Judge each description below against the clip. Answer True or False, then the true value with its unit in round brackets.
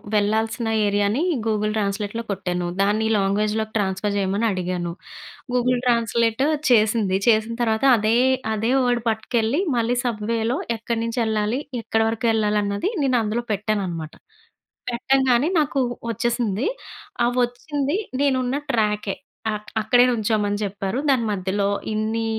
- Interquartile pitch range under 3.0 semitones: True (2.5 semitones)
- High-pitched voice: True (220 Hz)